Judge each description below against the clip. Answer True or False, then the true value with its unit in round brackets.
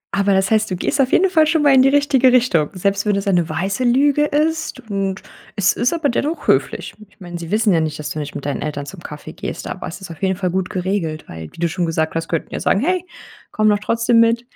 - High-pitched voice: True (200 Hz)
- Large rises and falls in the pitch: True (6.8 semitones)